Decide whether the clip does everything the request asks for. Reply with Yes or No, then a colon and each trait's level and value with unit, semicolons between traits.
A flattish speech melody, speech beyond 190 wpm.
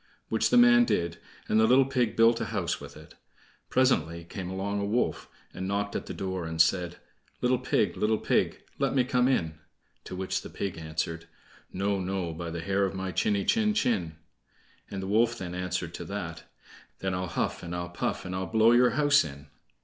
No: average, 5.0 semitones; average, 200 wpm